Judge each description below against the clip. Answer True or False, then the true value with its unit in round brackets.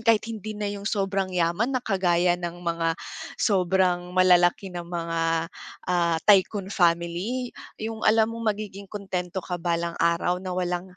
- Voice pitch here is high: False (180 Hz)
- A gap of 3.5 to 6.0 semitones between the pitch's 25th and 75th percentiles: False (2.9 semitones)